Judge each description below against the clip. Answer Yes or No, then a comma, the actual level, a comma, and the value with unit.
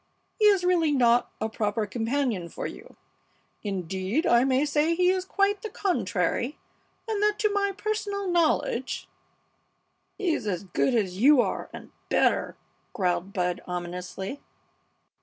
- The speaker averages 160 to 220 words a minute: No, average, 140 wpm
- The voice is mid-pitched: No, very high, 265 Hz